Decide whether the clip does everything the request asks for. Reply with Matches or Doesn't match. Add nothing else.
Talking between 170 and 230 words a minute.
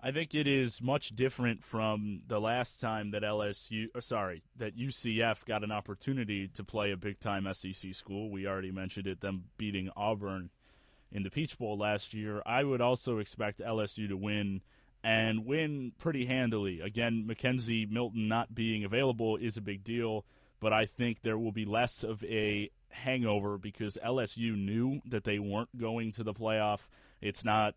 Matches